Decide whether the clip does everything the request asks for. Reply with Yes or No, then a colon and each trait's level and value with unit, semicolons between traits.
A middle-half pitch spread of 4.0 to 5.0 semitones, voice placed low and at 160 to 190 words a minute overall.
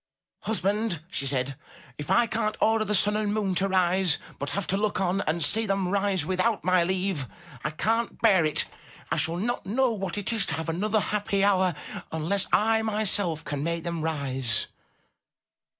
No: average, 4.3 semitones; high, 190 Hz; average, 180 wpm